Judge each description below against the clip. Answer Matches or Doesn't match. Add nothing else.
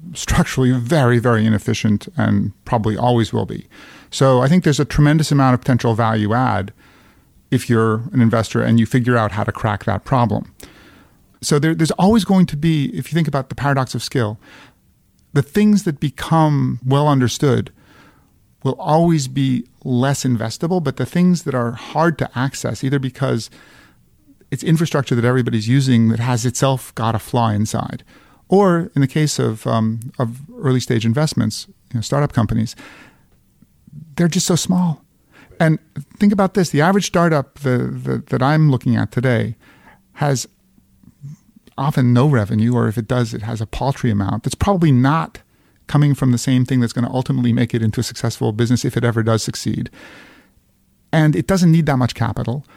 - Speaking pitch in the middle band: Doesn't match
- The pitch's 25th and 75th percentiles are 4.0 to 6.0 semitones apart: Matches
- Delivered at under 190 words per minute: Matches